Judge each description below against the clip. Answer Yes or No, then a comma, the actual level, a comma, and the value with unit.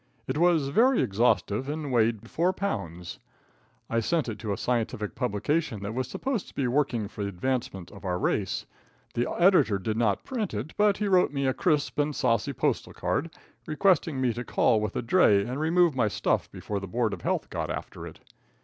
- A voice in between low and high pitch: No, low, 125 Hz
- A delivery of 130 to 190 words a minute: No, average, 200 wpm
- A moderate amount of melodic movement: No, wide, 6.8 semitones